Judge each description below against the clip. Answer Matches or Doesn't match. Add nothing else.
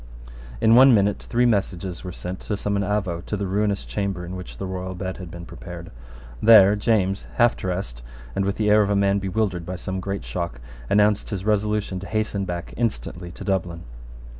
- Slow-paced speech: Doesn't match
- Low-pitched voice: Matches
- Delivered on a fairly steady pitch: Matches